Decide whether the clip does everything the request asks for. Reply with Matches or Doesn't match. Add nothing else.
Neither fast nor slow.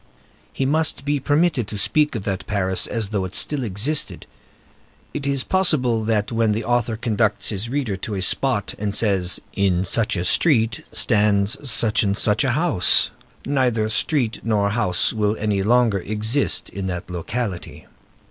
Matches